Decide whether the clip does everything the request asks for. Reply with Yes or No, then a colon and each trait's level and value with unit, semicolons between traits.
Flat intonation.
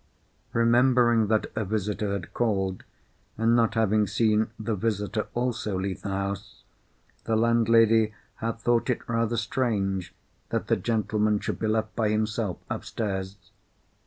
Yes: narrow, 2.0 semitones